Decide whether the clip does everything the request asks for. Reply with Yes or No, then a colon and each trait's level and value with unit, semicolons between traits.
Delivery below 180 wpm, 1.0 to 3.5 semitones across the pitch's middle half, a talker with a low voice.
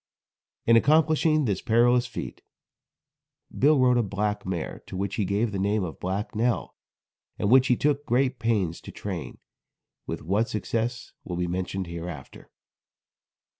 No: average, 150 wpm; average, 4.6 semitones; low, 110 Hz